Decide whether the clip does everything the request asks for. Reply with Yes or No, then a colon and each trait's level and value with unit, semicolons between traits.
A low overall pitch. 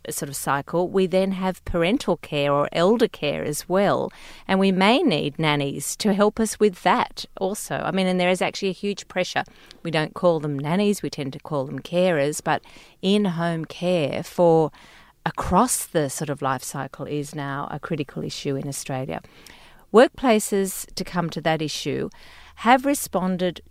No: medium, 175 Hz